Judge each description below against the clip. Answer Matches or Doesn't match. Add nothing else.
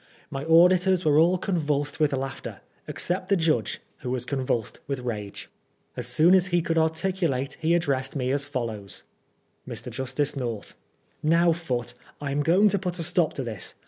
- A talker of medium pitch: Matches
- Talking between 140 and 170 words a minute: Doesn't match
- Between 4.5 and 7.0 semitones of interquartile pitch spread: Matches